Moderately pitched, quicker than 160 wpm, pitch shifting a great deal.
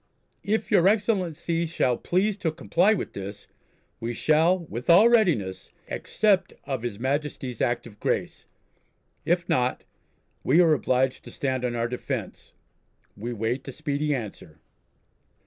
No: medium, 145 Hz; average, 140 wpm; wide, 6.4 semitones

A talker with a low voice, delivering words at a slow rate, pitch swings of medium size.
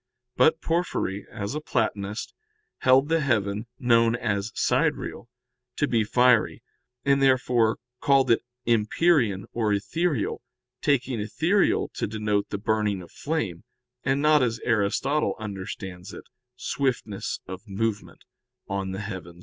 Yes: low, 115 Hz; slow, 125 wpm; average, 4.9 semitones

